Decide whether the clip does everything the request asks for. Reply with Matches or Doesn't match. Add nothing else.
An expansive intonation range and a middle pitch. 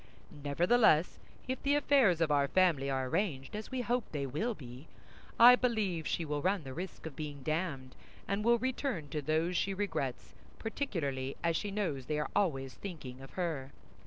Matches